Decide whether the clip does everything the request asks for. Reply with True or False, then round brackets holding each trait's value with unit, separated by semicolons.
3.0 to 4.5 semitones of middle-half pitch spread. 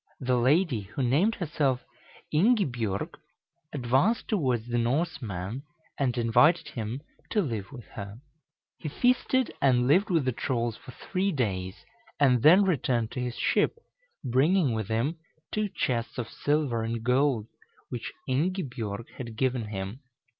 False (4.9 semitones)